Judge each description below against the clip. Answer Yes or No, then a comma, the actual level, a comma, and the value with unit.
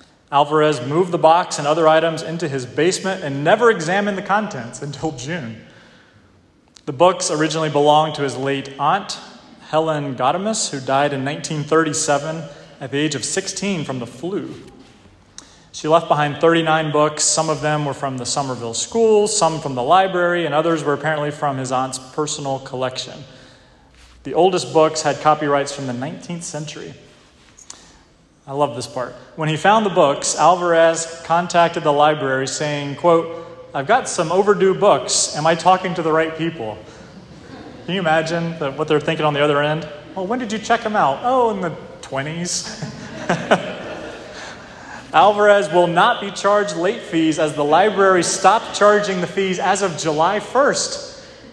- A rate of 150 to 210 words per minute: Yes, average, 165 wpm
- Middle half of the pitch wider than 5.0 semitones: No, average, 3.5 semitones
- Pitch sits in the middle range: Yes, medium, 155 Hz